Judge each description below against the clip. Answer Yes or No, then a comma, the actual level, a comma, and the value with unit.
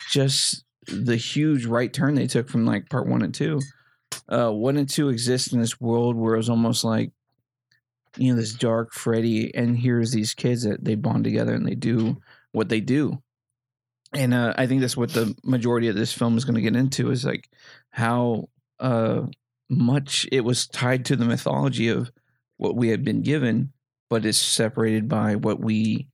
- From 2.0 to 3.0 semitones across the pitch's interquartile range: Yes, narrow, 2.5 semitones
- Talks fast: No, average, 195 wpm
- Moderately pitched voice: No, low, 120 Hz